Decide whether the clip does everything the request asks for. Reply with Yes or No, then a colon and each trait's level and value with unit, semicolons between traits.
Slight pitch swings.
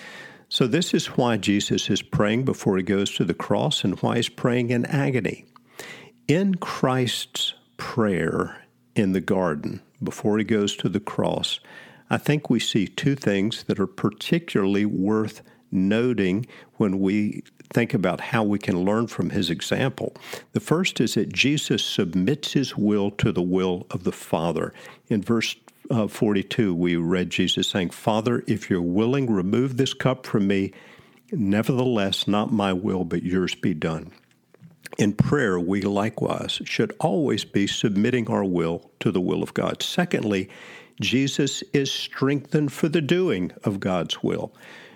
No: average, 5.1 semitones